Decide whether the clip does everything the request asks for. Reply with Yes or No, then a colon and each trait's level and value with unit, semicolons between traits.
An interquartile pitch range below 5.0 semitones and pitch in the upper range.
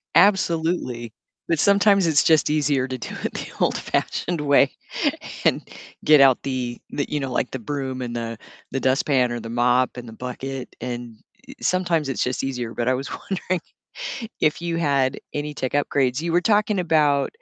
No: average, 4.4 semitones; low, 135 Hz